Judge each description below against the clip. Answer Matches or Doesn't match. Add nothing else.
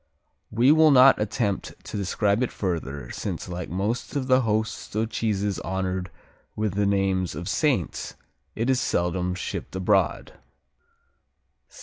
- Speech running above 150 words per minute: Doesn't match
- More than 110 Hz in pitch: Doesn't match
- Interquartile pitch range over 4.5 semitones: Doesn't match